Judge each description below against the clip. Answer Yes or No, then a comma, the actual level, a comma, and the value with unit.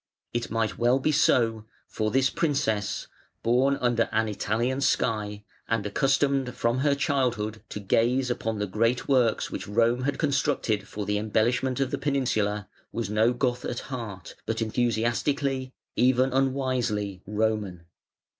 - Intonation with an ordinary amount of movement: Yes, average, 3.5 semitones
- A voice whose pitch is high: No, low, 120 Hz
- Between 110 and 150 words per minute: Yes, average, 145 wpm